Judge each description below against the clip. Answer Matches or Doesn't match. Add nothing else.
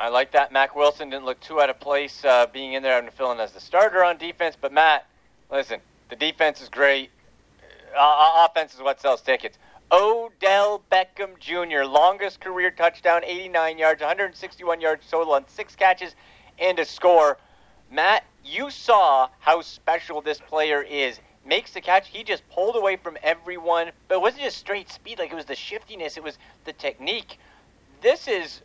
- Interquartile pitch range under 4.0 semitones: Doesn't match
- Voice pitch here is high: Doesn't match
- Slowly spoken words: Doesn't match